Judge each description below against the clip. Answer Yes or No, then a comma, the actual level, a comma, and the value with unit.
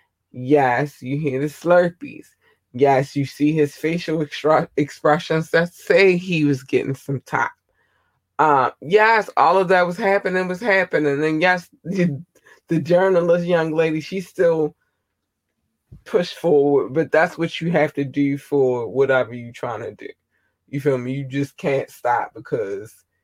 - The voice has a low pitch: No, medium, 155 Hz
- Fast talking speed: No, average, 150 wpm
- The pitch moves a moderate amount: Yes, average, 4.1 semitones